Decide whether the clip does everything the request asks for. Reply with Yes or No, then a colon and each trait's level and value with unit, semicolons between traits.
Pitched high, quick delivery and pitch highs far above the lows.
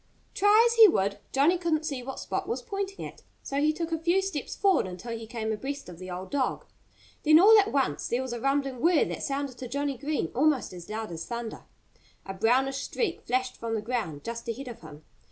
Yes: very high, 270 Hz; fast, 225 wpm; wide, 5.7 semitones